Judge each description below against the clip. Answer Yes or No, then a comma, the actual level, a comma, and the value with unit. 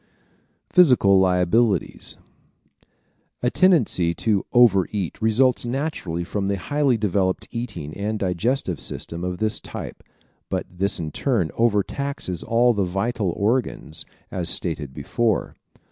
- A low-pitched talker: Yes, low, 100 Hz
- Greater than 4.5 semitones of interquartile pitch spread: Yes, average, 5.1 semitones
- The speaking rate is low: Yes, slow, 125 wpm